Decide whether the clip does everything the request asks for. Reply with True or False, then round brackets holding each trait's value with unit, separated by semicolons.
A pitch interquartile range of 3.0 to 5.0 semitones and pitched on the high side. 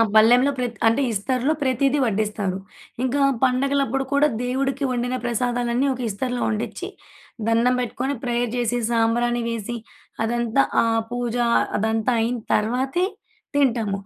False (2.4 semitones; 245 Hz)